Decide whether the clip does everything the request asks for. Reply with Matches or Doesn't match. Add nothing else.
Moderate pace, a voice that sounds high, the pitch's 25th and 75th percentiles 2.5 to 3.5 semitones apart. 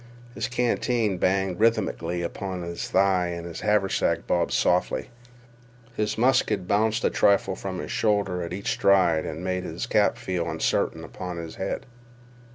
Doesn't match